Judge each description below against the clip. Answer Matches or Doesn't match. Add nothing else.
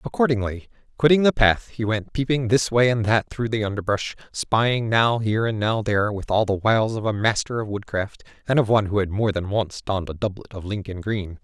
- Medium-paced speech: Doesn't match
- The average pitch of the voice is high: Doesn't match